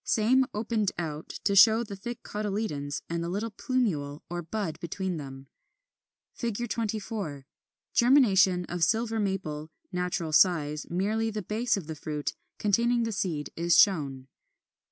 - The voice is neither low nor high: No, high, 195 Hz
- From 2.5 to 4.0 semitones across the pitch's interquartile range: No, wide, 5.6 semitones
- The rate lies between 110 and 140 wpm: Yes, slow, 135 wpm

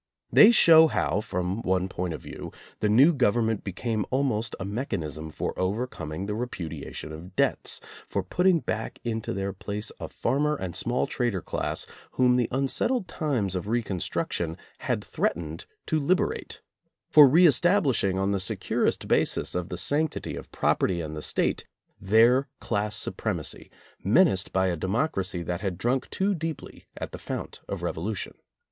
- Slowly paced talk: No, average, 155 wpm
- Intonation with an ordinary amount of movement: No, wide, 6.3 semitones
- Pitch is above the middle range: No, low, 105 Hz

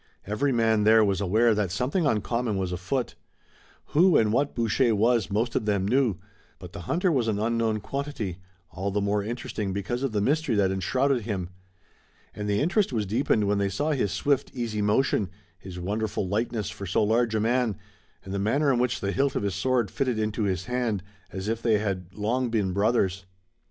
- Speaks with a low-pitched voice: Yes, low, 110 Hz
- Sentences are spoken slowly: No, average, 195 wpm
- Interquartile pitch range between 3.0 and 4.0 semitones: Yes, average, 3.7 semitones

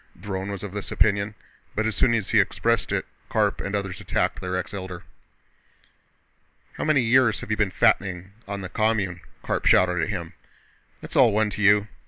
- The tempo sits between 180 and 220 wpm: Yes, average, 190 wpm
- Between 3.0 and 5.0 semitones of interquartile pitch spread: No, narrow, 2.5 semitones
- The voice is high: No, low, 100 Hz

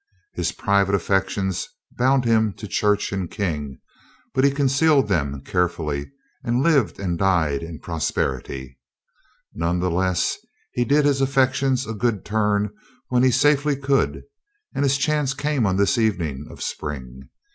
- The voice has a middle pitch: No, low, 105 Hz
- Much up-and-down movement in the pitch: Yes, wide, 7.7 semitones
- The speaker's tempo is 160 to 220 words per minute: No, average, 145 wpm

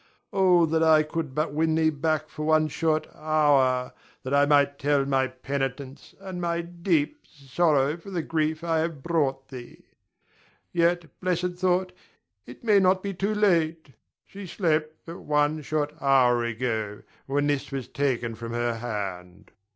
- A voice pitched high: No, medium, 155 Hz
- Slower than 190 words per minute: Yes, average, 160 wpm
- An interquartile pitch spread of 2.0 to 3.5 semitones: No, average, 3.9 semitones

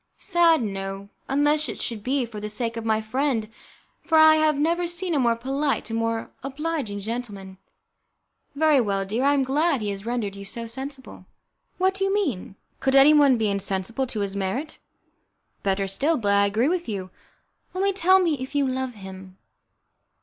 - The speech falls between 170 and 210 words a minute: Yes, average, 180 wpm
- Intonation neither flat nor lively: No, wide, 6.5 semitones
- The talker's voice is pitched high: Yes, very high, 250 Hz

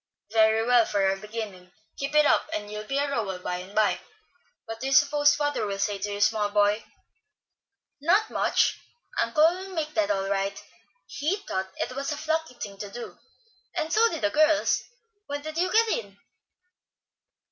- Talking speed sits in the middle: Yes, average, 185 wpm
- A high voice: Yes, high, 235 Hz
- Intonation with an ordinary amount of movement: No, wide, 6.9 semitones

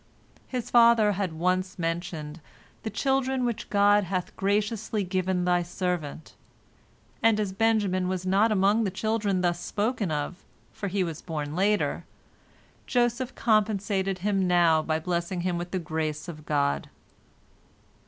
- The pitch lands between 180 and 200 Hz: Yes, high, 190 Hz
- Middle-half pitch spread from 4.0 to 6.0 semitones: No, average, 3.4 semitones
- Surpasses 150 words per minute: No, average, 145 wpm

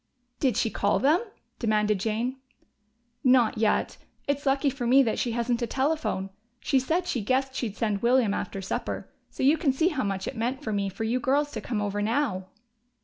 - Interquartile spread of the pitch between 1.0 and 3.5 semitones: No, average, 4.1 semitones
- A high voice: Yes, high, 240 Hz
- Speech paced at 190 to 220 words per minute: Yes, average, 200 wpm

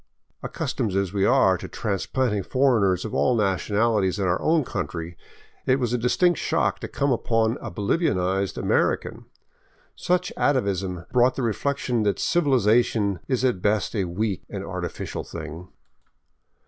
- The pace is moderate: Yes, average, 150 wpm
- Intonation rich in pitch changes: No, average, 5.0 semitones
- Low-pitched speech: Yes, low, 110 Hz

